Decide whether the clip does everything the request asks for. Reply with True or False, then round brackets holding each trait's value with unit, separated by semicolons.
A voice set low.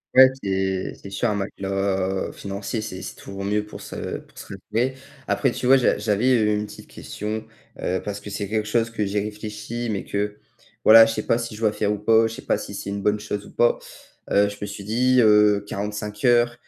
True (105 Hz)